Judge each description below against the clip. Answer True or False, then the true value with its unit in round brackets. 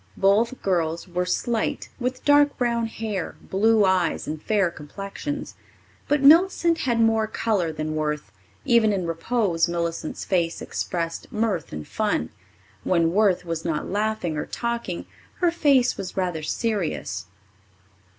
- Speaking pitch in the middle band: False (195 Hz)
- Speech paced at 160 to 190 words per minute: False (135 wpm)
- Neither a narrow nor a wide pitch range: False (5.8 semitones)